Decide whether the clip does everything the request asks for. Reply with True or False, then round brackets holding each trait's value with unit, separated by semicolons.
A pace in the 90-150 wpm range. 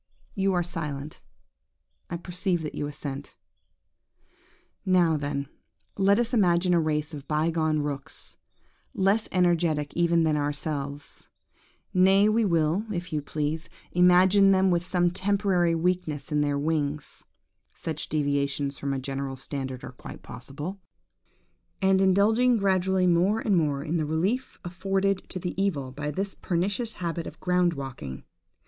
True (140 wpm)